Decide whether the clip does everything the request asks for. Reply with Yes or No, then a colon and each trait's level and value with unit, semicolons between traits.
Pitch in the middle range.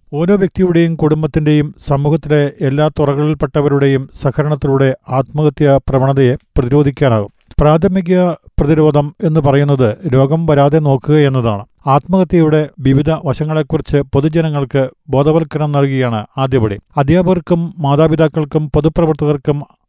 Yes: medium, 150 Hz